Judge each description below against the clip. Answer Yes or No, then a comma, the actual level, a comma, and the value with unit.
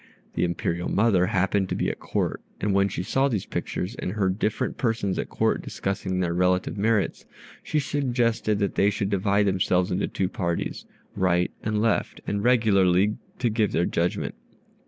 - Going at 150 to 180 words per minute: Yes, average, 175 wpm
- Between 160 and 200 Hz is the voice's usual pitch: No, low, 100 Hz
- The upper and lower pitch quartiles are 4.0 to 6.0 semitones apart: No, average, 2.8 semitones